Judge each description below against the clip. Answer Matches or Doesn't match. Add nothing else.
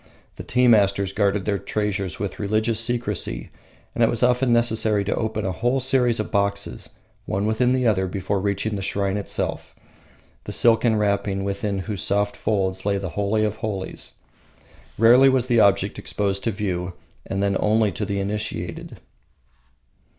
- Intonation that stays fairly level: Matches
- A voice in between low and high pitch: Doesn't match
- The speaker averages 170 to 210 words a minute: Doesn't match